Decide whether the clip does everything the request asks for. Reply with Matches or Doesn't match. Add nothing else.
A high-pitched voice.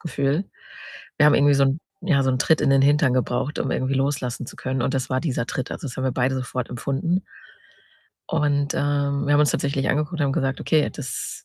Doesn't match